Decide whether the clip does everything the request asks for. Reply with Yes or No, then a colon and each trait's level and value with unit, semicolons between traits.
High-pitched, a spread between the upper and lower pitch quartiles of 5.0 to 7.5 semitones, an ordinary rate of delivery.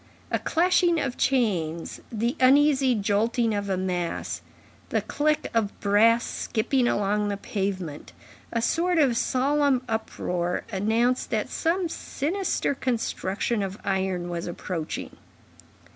No: high, 225 Hz; wide, 5.6 semitones; slow, 120 wpm